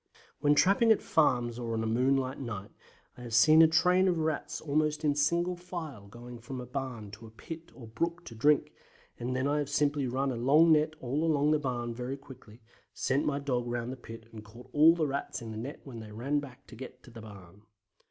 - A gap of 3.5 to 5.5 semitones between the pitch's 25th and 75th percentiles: Yes, average, 4.3 semitones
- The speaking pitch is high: No, low, 135 Hz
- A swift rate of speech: Yes, fast, 225 wpm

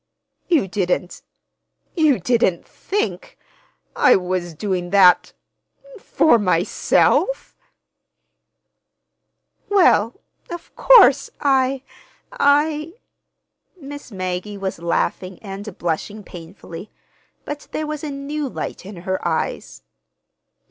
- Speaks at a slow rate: Yes, slow, 80 wpm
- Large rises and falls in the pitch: Yes, wide, 8.4 semitones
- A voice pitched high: Yes, high, 220 Hz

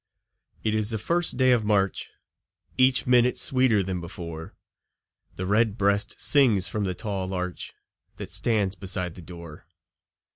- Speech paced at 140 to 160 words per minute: Yes, average, 145 wpm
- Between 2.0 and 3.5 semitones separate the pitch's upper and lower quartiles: No, average, 4.2 semitones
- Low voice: Yes, low, 100 Hz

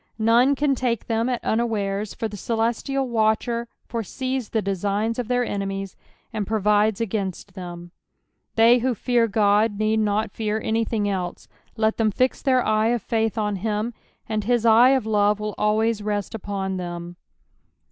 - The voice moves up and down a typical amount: No, narrow, 2.3 semitones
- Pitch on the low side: No, high, 220 Hz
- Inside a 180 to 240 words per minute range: No, average, 165 wpm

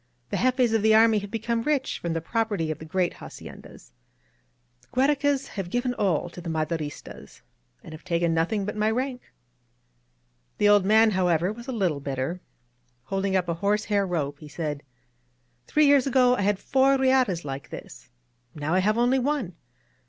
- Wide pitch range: Yes, wide, 6.6 semitones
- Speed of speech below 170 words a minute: No, average, 190 wpm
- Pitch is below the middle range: No, high, 200 Hz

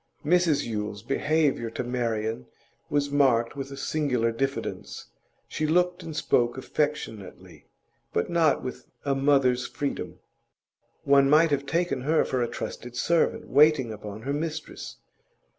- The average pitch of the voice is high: No, low, 135 Hz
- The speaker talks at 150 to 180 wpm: No, slow, 135 wpm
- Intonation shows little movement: No, average, 4.2 semitones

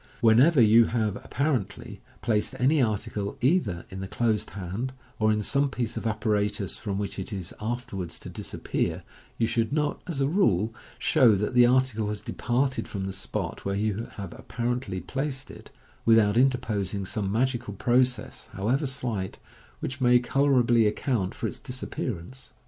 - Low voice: Yes, low, 115 Hz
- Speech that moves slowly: No, average, 160 wpm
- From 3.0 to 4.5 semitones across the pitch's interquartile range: Yes, average, 4.0 semitones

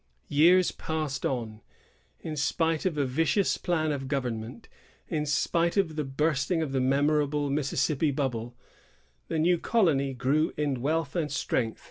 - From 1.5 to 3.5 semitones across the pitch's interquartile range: Yes, average, 3.1 semitones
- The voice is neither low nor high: Yes, medium, 150 Hz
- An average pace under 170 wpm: Yes, average, 145 wpm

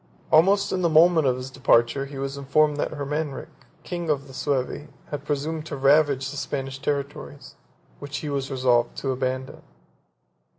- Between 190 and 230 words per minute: No, average, 165 wpm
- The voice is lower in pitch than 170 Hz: Yes, medium, 140 Hz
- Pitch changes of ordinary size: No, narrow, 2.1 semitones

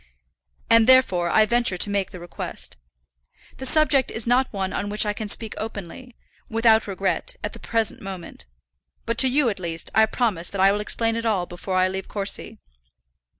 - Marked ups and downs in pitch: No, average, 3.4 semitones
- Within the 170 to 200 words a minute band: Yes, average, 190 wpm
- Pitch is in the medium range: No, high, 215 Hz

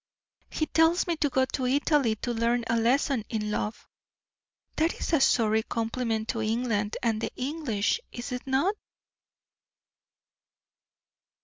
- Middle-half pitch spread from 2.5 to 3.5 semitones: No, average, 3.9 semitones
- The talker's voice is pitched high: Yes, high, 245 Hz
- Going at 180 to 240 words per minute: No, slow, 135 wpm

